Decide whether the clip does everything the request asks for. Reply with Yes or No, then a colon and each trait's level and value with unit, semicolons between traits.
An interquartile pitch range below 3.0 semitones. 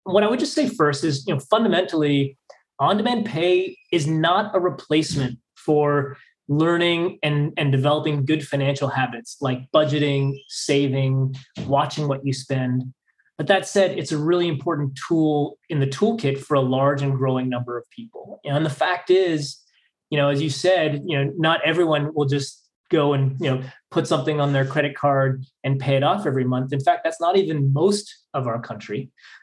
No: average, 3.8 semitones